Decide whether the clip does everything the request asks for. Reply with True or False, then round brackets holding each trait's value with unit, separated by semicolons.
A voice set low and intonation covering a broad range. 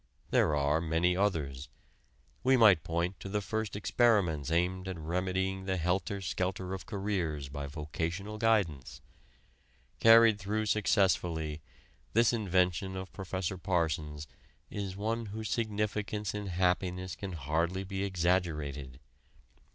False (95 Hz; 3.8 semitones)